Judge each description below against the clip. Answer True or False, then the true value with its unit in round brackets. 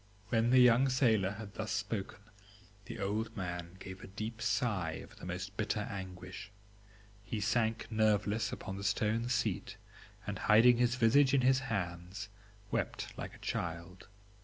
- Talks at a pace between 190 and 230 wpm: False (155 wpm)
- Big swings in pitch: False (3.4 semitones)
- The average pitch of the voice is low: True (105 Hz)